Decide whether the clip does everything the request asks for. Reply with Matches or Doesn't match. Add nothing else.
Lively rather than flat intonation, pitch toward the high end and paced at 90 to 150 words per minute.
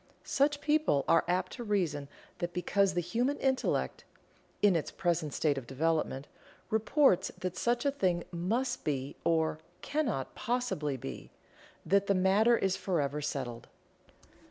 Doesn't match